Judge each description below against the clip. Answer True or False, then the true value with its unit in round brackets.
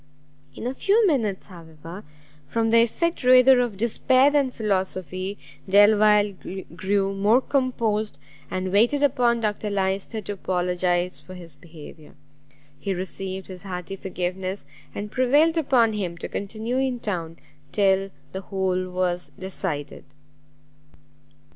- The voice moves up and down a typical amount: True (4.2 semitones)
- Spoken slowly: True (125 wpm)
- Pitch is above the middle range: True (200 Hz)